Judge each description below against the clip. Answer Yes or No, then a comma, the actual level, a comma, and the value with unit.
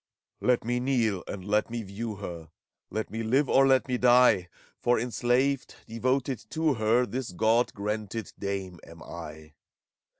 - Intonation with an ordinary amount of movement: Yes, average, 4.0 semitones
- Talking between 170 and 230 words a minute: No, average, 155 wpm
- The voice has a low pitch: Yes, low, 115 Hz